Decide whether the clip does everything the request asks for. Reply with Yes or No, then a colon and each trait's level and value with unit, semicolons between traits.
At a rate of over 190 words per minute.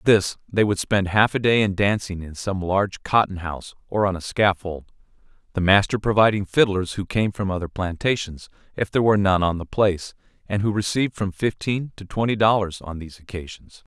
Yes: average, 200 wpm